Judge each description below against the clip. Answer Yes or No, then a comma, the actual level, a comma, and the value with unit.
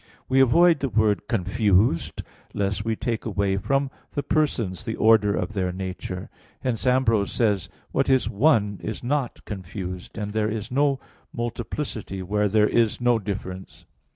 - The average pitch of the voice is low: Yes, low, 110 Hz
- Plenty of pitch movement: No, average, 4.0 semitones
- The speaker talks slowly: No, average, 165 wpm